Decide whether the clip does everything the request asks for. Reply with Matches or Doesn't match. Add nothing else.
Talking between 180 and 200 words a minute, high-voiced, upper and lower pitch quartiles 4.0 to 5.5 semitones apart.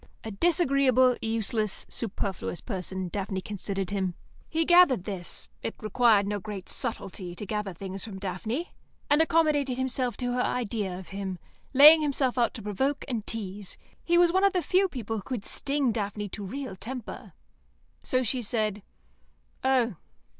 Doesn't match